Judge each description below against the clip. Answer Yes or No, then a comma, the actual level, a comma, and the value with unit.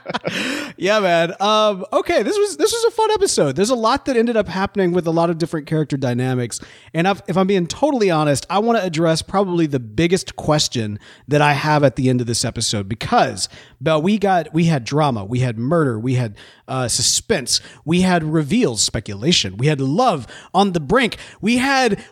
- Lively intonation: Yes, wide, 7.6 semitones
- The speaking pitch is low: No, medium, 165 Hz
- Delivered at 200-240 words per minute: Yes, fast, 205 wpm